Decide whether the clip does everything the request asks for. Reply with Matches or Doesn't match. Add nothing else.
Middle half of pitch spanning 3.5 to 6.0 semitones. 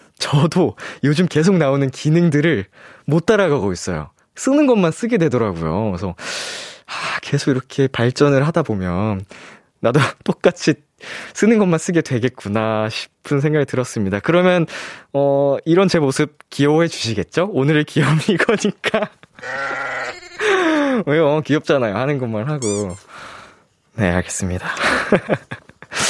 Doesn't match